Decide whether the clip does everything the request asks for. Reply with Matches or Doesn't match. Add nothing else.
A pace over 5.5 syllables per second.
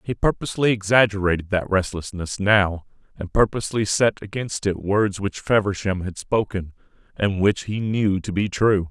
Doesn't match